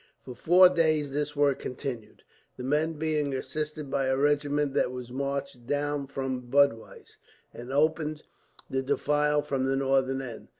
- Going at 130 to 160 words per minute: Yes, average, 155 wpm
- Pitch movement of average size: No, narrow, 2.0 semitones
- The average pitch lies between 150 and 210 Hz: No, medium, 140 Hz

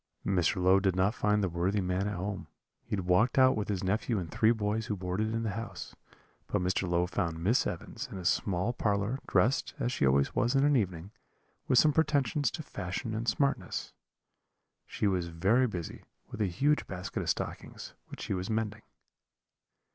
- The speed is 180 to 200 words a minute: Yes, average, 190 wpm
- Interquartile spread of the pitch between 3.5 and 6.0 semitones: Yes, average, 3.9 semitones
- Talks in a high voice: No, low, 105 Hz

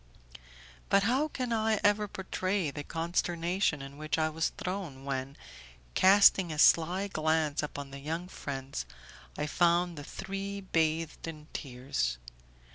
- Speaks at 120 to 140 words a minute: Yes, slow, 135 wpm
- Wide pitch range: No, average, 4.7 semitones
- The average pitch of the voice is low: No, medium, 165 Hz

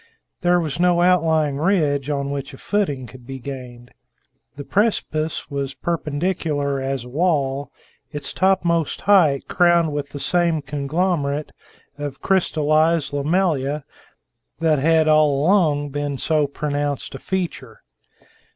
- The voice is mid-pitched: Yes, medium, 150 Hz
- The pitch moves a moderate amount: Yes, average, 3.3 semitones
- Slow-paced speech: Yes, slow, 125 wpm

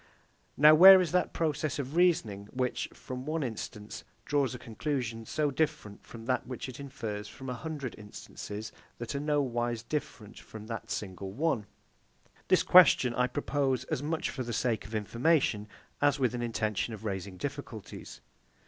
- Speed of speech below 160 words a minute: No, average, 165 wpm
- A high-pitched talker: No, low, 125 Hz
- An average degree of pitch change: Yes, average, 4.9 semitones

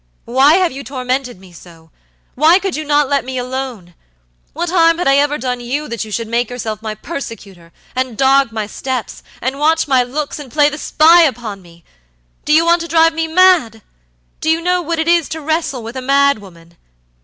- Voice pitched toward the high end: Yes, very high, 270 Hz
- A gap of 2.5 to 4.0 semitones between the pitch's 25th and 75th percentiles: No, wide, 5.5 semitones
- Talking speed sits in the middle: No, fast, 210 wpm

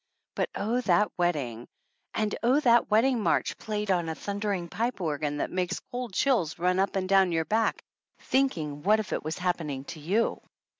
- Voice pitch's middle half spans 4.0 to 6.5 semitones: Yes, average, 5.0 semitones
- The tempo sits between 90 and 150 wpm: No, average, 185 wpm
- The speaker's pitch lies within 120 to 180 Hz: No, high, 190 Hz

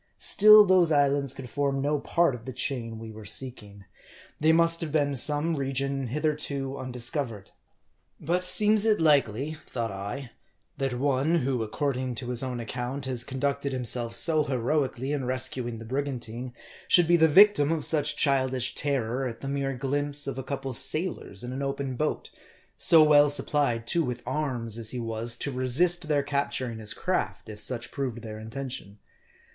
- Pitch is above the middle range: No, low, 135 Hz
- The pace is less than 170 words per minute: No, average, 175 wpm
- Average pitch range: Yes, average, 3.2 semitones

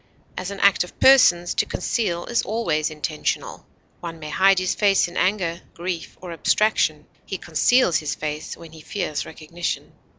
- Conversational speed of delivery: Yes, average, 165 wpm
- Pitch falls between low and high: Yes, medium, 175 Hz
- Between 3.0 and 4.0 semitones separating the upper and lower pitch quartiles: Yes, average, 3.7 semitones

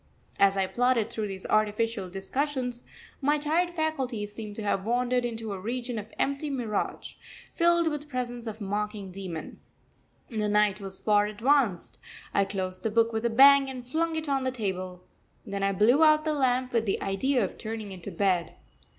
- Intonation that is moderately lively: Yes, average, 4.8 semitones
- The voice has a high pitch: Yes, high, 225 Hz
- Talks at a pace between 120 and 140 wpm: No, average, 185 wpm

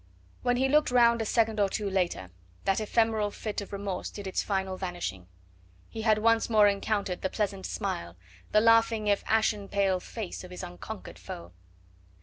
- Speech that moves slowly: No, average, 175 wpm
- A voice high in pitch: Yes, high, 205 Hz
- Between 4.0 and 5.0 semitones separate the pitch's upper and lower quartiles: No, average, 2.8 semitones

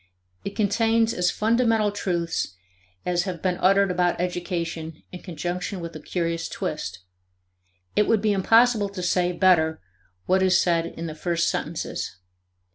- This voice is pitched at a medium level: Yes, medium, 180 Hz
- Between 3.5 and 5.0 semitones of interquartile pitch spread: No, average, 3.1 semitones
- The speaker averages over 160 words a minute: No, average, 145 wpm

